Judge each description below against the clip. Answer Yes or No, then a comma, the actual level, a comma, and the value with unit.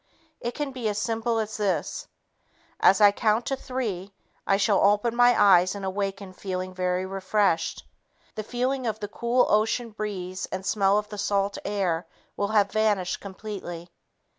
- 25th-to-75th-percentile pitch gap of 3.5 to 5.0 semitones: No, narrow, 2.5 semitones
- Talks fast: No, average, 165 wpm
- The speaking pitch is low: No, high, 205 Hz